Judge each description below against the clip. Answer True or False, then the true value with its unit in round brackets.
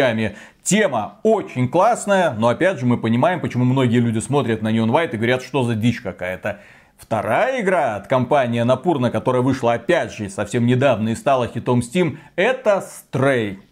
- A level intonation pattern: False (3.2 semitones)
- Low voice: True (120 Hz)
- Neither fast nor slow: False (165 wpm)